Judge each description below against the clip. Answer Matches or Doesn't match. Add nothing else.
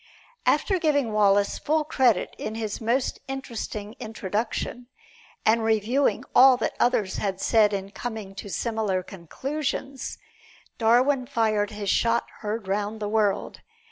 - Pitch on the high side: Matches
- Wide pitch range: Doesn't match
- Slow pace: Matches